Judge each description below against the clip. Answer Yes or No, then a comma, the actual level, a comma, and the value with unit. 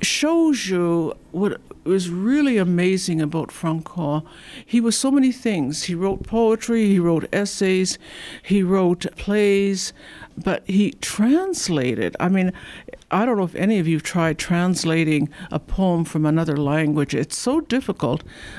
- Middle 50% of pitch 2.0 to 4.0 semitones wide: No, average, 4.7 semitones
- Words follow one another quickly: No, average, 145 wpm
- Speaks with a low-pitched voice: No, medium, 185 Hz